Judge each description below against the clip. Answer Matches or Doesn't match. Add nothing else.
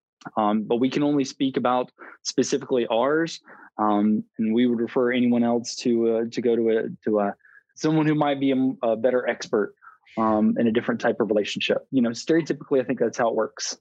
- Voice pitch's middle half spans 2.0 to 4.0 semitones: Matches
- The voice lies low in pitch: Matches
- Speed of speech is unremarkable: Doesn't match